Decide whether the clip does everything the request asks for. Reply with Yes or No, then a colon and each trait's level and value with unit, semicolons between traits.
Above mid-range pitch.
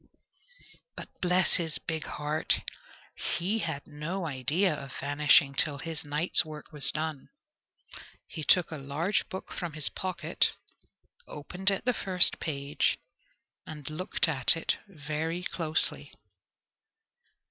No: medium, 155 Hz